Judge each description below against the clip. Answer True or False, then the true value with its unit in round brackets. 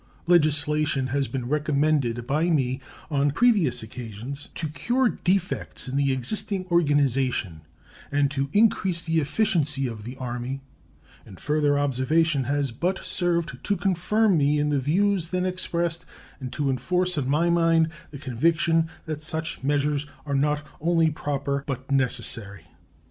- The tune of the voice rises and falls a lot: False (3.9 semitones)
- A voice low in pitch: False (145 Hz)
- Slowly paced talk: False (145 wpm)